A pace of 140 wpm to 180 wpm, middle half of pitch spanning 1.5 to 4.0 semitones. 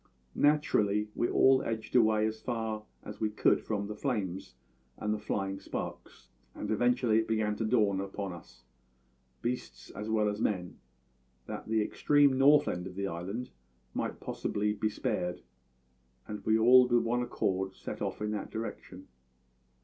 Yes: average, 165 wpm; average, 3.0 semitones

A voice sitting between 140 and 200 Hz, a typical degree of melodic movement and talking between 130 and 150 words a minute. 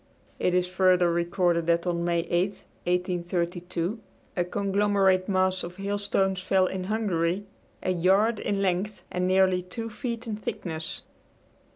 No: medium, 185 Hz; narrow, 2.1 semitones; average, 140 wpm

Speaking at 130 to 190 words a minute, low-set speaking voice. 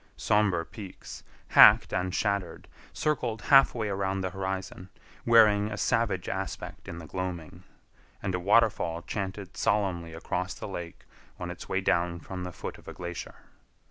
Yes: average, 155 wpm; very low, 95 Hz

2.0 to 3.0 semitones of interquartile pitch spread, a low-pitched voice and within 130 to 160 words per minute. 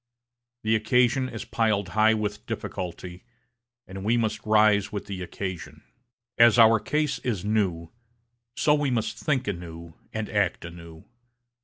No: average, 3.6 semitones; low, 105 Hz; average, 140 wpm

